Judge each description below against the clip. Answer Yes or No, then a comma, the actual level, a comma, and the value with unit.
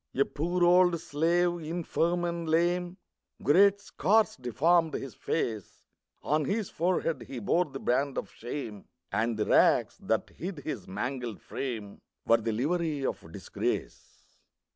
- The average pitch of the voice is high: No, medium, 155 Hz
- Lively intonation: Yes, wide, 6.0 semitones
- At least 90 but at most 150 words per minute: Yes, average, 140 wpm